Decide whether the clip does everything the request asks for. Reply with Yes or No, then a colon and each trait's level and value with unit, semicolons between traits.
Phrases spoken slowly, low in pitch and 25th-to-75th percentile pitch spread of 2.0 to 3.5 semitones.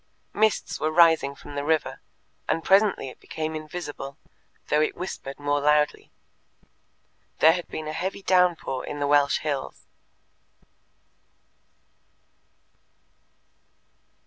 No: slow, 110 wpm; medium, 155 Hz; average, 3.1 semitones